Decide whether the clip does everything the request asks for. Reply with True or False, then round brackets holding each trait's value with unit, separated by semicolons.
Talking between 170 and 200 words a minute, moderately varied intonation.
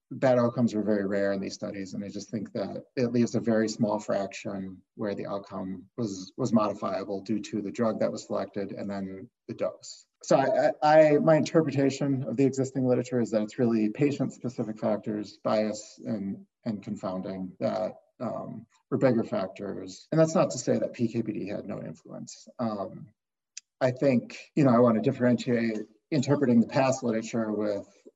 True (180 wpm; 4.2 semitones)